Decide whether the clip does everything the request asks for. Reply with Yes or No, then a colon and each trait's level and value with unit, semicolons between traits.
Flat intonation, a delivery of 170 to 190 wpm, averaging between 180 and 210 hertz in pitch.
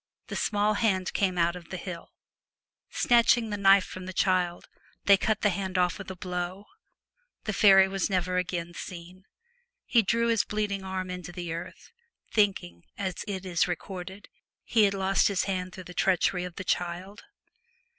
Yes: narrow, 2.0 semitones; average, 175 wpm; high, 190 Hz